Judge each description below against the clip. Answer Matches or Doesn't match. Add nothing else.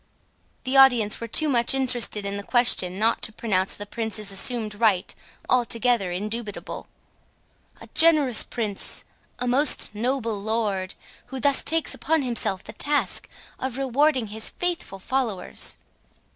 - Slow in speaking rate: Matches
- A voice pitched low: Doesn't match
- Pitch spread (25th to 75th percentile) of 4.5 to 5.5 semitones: Doesn't match